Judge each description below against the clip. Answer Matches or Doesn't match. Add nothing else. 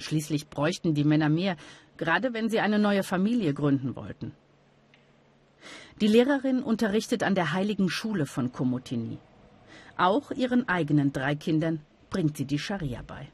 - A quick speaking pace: Doesn't match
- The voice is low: Doesn't match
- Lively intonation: Matches